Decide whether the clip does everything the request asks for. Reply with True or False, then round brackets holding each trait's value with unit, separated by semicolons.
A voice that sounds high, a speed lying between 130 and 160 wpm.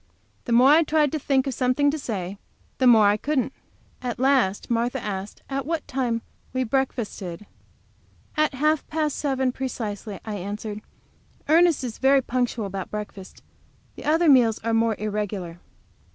True (245 Hz; 155 wpm)